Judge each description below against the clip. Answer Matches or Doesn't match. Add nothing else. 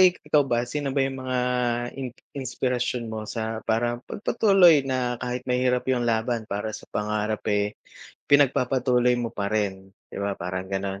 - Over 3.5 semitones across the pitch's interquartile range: Doesn't match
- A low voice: Matches